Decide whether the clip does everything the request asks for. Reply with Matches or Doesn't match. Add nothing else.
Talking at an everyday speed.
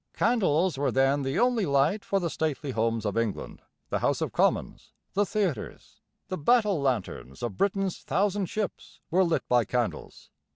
Matches